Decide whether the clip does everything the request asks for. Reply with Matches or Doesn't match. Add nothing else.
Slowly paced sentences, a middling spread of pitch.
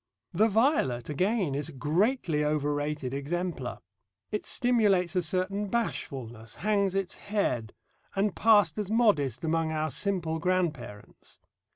Doesn't match